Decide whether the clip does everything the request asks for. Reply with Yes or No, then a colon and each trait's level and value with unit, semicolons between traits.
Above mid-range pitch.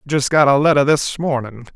No: medium, 140 Hz